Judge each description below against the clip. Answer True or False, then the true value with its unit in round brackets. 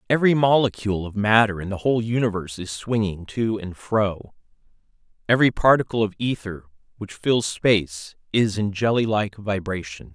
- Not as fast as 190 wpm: True (150 wpm)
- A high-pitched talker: False (105 Hz)